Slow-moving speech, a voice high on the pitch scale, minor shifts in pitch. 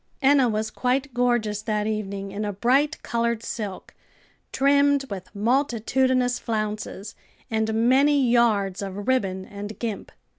No: slow, 125 wpm; high, 225 Hz; average, 3.7 semitones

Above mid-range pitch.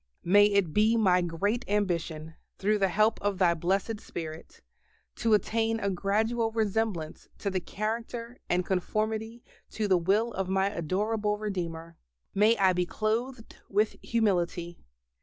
Yes: high, 205 Hz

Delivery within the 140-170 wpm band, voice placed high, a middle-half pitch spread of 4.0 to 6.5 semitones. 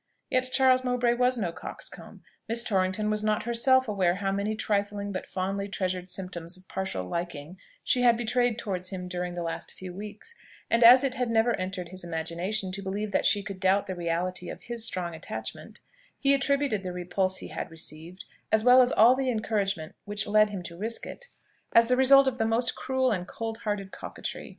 No: average, 200 wpm; high, 200 Hz; average, 4.3 semitones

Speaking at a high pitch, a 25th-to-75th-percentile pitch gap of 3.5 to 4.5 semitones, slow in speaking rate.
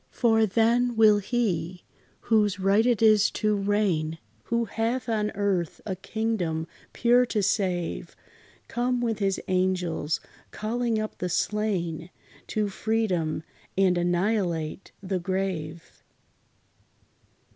Yes: high, 200 Hz; average, 3.8 semitones; slow, 115 wpm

